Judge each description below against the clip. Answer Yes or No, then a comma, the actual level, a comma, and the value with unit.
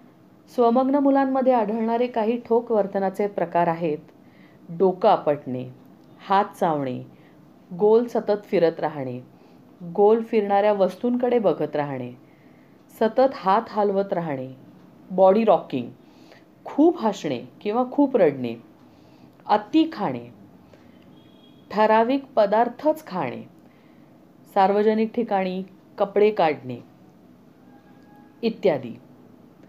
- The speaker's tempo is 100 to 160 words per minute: No, average, 85 wpm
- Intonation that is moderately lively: No, wide, 7.1 semitones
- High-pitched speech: Yes, high, 200 Hz